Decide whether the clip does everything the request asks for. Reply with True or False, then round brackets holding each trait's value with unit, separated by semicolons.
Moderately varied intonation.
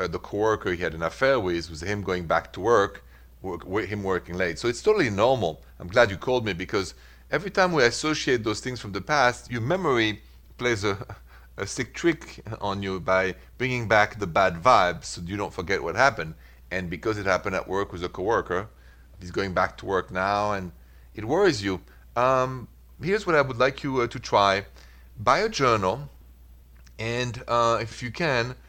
False (7.0 semitones)